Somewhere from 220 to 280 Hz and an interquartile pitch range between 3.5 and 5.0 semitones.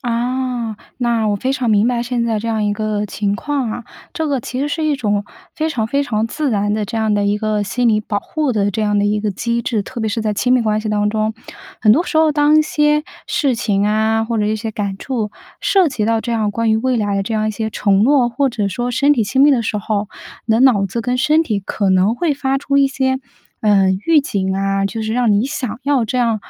Yes: high, 225 Hz; average, 3.8 semitones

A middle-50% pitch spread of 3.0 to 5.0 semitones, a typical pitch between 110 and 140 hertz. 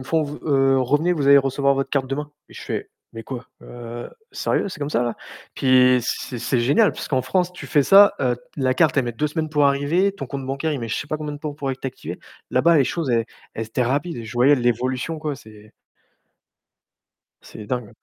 Yes: average, 3.3 semitones; low, 135 Hz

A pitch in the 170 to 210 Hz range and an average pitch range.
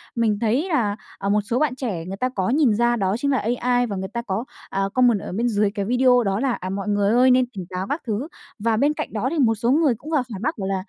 No: high, 230 Hz; average, 4.1 semitones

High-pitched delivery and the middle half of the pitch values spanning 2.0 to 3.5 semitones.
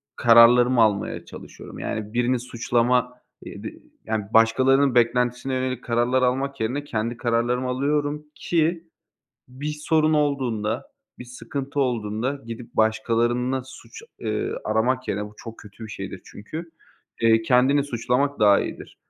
No: low, 125 Hz; average, 2.8 semitones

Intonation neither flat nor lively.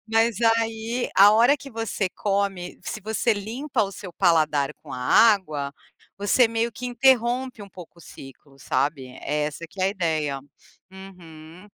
No: wide, 6.2 semitones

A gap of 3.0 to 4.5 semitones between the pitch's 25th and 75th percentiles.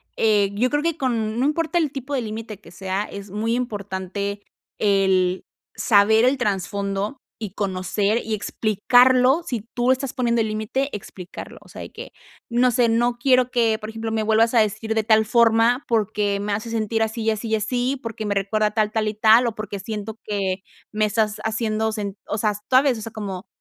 No: narrow, 2.6 semitones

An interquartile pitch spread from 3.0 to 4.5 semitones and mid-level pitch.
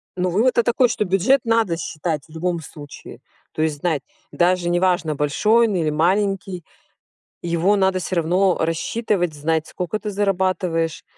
Yes: average, 3.3 semitones; medium, 180 Hz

